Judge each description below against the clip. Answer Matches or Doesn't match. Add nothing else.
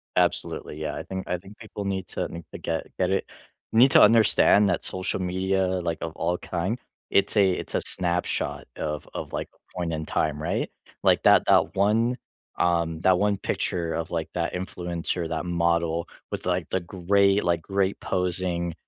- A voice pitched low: Matches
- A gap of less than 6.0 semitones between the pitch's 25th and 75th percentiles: Matches